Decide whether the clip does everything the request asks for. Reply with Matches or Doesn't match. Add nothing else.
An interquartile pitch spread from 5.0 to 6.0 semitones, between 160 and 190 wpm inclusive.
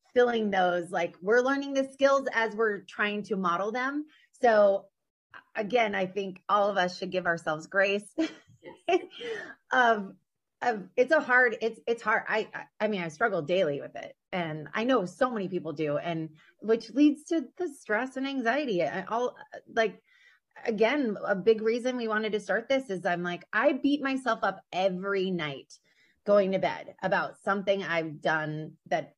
Matches